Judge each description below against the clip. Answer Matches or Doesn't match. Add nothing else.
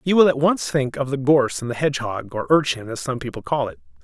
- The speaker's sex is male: Matches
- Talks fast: Matches